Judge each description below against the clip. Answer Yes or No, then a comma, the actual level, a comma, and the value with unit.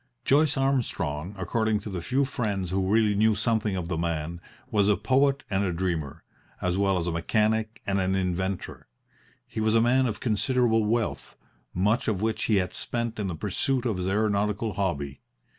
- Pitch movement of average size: Yes, average, 3.5 semitones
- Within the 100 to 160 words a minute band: No, average, 185 wpm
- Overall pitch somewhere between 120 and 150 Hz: No, low, 105 Hz